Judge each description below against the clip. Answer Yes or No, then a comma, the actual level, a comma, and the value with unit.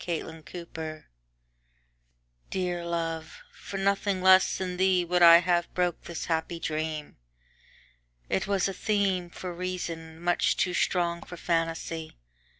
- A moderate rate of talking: No, slow, 115 wpm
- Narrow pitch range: Yes, narrow, 2.1 semitones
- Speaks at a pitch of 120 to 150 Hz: No, medium, 175 Hz